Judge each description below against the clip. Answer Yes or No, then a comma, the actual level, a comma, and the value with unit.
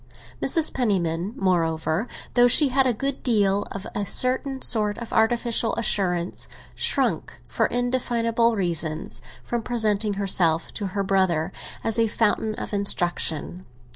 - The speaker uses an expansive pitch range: No, average, 4.3 semitones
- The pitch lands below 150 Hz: No, high, 210 Hz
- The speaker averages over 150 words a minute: No, slow, 135 wpm